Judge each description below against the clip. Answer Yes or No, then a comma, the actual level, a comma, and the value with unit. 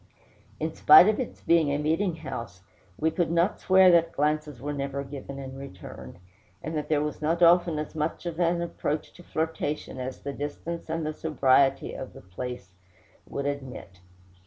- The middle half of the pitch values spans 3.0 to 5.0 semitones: Yes, average, 3.3 semitones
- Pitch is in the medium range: Yes, medium, 150 Hz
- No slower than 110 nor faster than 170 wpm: No, average, 180 wpm